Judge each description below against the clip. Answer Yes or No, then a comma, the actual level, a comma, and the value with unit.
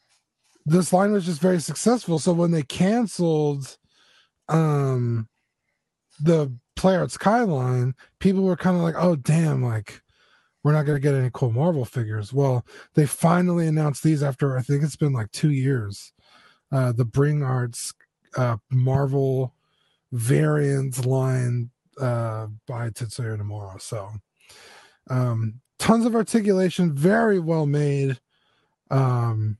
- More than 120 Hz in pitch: Yes, medium, 140 Hz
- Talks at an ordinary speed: No, slow, 130 wpm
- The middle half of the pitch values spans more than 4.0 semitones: Yes, average, 5.0 semitones